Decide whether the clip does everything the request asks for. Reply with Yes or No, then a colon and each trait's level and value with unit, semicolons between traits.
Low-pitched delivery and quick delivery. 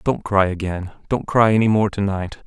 Yes: low, 100 Hz; fast, 220 wpm